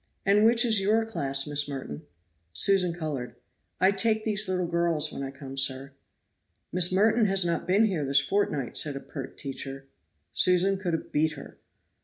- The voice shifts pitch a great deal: Yes, wide, 6.2 semitones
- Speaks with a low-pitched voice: No, medium, 170 Hz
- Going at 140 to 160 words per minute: No, average, 175 wpm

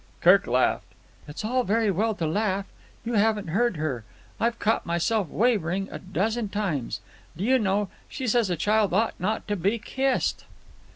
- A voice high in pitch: Yes, high, 210 Hz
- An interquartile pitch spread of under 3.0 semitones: No, average, 3.5 semitones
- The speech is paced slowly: No, average, 170 wpm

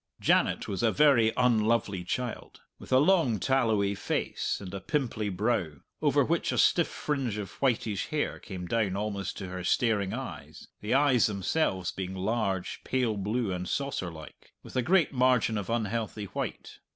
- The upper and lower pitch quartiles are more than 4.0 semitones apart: Yes, average, 4.4 semitones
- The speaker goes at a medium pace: Yes, average, 165 wpm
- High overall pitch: No, low, 110 Hz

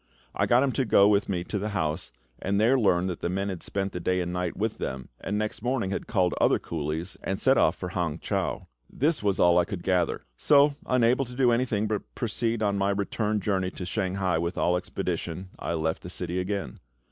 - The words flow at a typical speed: No, fast, 225 wpm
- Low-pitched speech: Yes, very low, 95 Hz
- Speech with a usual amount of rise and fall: Yes, average, 3.4 semitones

